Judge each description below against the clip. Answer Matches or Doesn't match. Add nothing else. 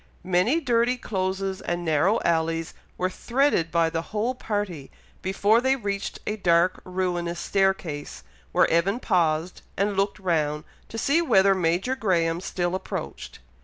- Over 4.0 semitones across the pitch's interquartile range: Doesn't match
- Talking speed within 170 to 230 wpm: Doesn't match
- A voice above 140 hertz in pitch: Matches